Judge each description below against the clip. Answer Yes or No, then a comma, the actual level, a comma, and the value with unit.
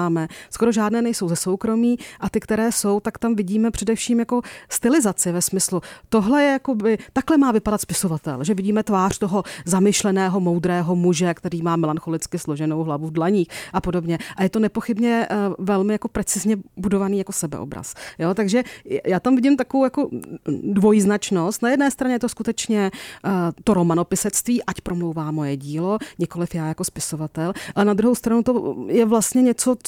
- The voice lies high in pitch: Yes, high, 200 Hz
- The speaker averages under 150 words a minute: No, average, 165 wpm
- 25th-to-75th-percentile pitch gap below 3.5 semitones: No, average, 4.6 semitones